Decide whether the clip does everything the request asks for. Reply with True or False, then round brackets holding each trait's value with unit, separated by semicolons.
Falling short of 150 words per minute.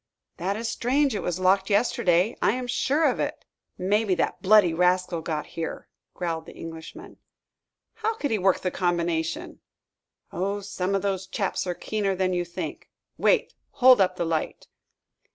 False (165 wpm)